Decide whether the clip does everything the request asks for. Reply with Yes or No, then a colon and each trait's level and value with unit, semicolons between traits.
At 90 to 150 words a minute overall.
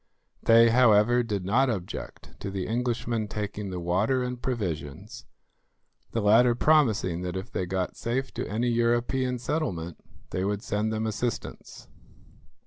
Yes: average, 140 wpm